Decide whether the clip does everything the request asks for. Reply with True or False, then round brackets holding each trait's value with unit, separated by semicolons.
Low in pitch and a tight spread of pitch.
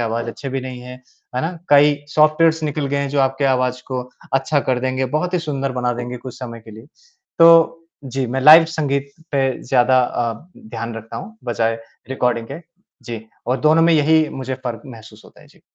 False (130 Hz; 3.1 semitones)